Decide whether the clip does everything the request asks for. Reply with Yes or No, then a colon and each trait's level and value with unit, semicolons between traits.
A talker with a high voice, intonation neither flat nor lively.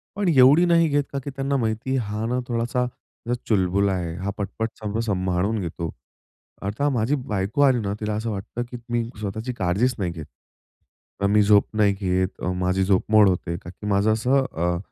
No: low, 105 Hz; average, 4.4 semitones